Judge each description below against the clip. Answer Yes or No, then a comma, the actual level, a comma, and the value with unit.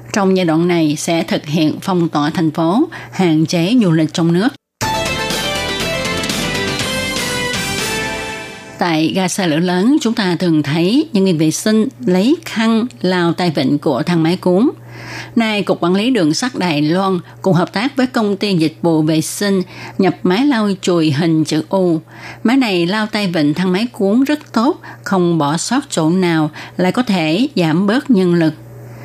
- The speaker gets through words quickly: No, average, 180 wpm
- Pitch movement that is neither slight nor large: Yes, average, 4.5 semitones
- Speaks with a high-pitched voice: No, medium, 180 Hz